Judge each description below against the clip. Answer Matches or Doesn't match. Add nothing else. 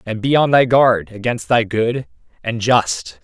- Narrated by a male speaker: Matches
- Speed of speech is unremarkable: Matches